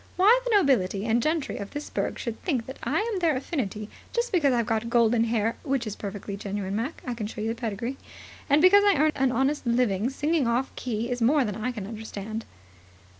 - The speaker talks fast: Yes, fast, 220 wpm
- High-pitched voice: Yes, high, 240 Hz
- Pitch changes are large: No, average, 4.9 semitones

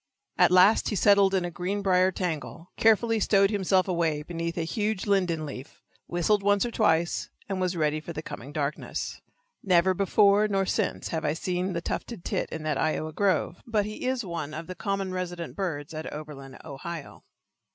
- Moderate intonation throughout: Yes, average, 3.7 semitones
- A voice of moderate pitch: Yes, medium, 180 Hz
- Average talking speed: Yes, average, 185 wpm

